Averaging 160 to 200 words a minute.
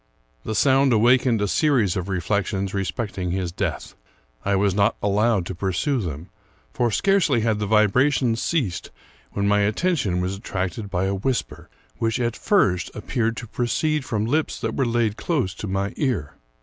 Yes: average, 170 wpm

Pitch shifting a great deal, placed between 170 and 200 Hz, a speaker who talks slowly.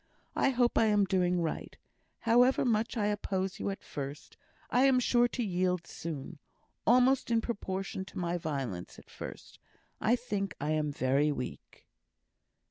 No: wide, 6.7 semitones; high, 190 Hz; average, 155 wpm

